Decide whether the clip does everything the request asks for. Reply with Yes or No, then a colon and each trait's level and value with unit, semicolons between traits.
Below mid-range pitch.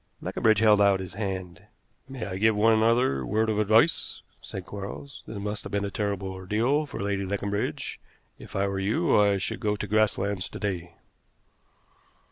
Yes: low, 100 Hz